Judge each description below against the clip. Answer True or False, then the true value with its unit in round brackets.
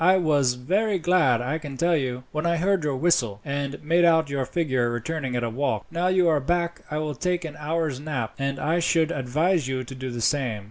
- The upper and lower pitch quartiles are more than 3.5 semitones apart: True (4.4 semitones)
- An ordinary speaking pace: False (230 wpm)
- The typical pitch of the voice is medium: True (150 Hz)